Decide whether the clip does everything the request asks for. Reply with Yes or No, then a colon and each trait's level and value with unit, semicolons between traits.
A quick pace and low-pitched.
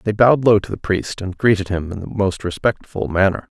Yes: fast, 235 wpm; low, 100 Hz